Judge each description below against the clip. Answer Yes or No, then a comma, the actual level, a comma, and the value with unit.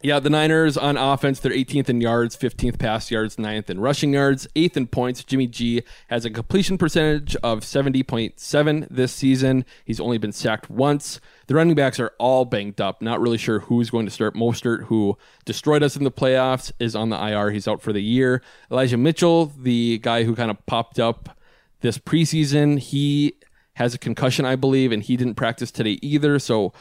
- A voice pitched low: Yes, low, 125 Hz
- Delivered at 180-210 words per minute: Yes, average, 195 wpm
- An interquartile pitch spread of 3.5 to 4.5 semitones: Yes, average, 3.8 semitones